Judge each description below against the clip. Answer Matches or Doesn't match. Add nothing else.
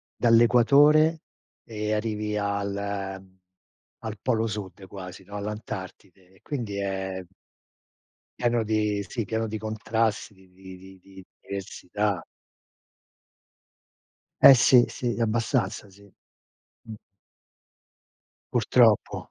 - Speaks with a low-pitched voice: Matches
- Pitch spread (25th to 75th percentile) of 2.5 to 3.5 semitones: Matches